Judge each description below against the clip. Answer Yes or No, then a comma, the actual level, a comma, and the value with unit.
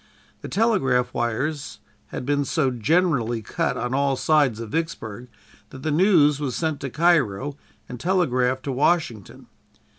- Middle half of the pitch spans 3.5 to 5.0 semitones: Yes, average, 4.3 semitones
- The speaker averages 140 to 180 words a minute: Yes, average, 145 wpm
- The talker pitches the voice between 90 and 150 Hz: Yes, low, 135 Hz